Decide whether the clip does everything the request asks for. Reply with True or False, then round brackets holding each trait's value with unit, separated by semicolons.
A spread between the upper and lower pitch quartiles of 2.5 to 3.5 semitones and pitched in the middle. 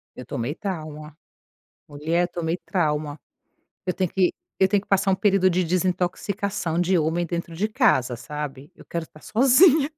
False (3.9 semitones; 175 Hz)